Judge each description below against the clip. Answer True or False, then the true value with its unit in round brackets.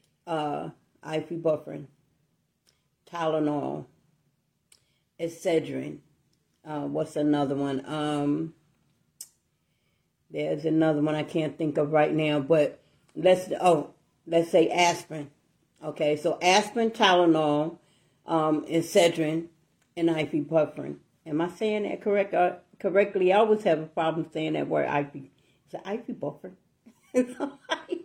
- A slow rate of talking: True (110 wpm)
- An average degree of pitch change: True (3.0 semitones)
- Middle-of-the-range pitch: True (160 Hz)